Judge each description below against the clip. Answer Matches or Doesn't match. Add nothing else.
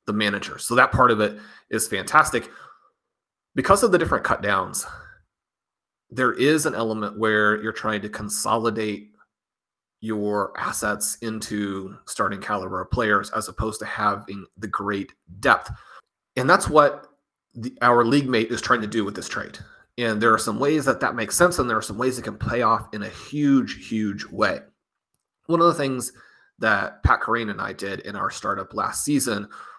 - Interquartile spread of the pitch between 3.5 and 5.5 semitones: Doesn't match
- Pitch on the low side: Matches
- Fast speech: Doesn't match